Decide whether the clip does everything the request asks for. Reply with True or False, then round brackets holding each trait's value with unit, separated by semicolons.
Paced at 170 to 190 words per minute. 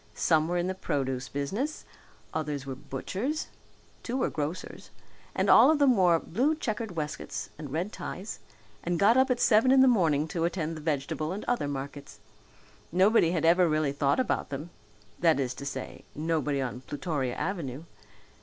True (175 wpm)